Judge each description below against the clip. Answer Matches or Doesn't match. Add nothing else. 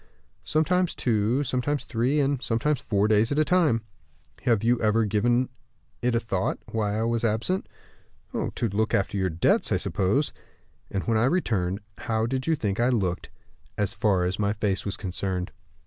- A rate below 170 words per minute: Doesn't match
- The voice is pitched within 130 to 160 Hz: Doesn't match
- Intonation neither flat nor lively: Matches